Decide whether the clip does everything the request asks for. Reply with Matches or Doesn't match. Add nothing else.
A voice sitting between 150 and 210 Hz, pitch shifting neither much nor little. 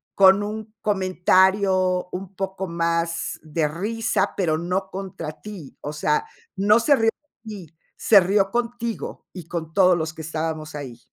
Matches